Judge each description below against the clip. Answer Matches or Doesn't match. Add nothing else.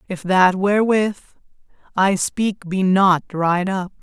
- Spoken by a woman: Matches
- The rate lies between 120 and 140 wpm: Matches